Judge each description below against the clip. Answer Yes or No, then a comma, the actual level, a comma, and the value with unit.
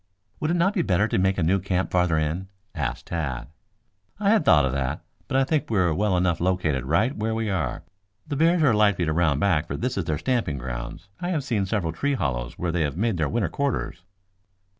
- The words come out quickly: Yes, fast, 230 wpm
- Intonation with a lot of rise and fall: Yes, wide, 7.1 semitones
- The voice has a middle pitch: No, very low, 90 Hz